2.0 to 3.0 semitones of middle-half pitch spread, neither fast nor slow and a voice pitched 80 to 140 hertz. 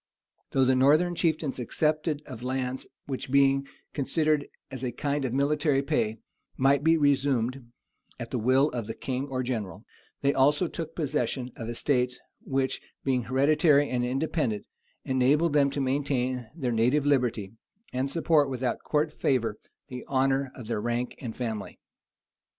Yes: narrow, 2.6 semitones; average, 150 wpm; low, 135 Hz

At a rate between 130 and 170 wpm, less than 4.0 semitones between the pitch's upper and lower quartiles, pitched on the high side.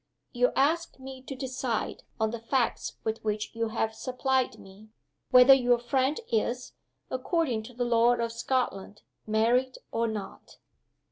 Yes: average, 145 wpm; average, 2.7 semitones; high, 245 Hz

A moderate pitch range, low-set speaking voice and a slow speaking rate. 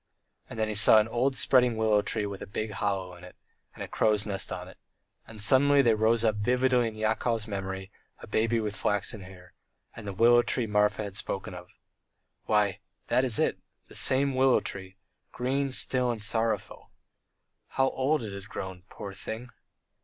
No: average, 3.3 semitones; low, 110 Hz; average, 185 wpm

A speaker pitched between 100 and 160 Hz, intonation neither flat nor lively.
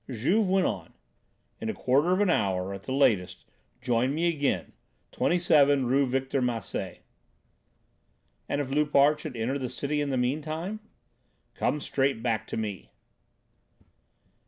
Yes: medium, 140 Hz; average, 3.8 semitones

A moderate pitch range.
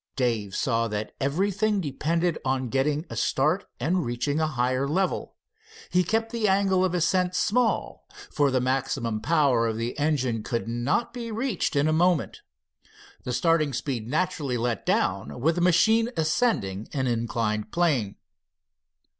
No: wide, 6.9 semitones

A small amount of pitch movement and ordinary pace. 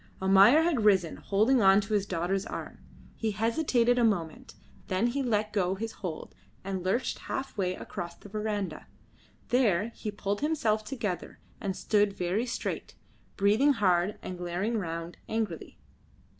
No: average, 3.6 semitones; average, 150 wpm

